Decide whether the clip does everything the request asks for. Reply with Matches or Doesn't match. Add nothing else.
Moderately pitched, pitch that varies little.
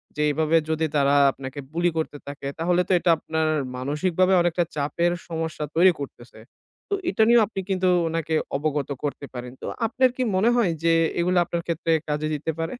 Doesn't match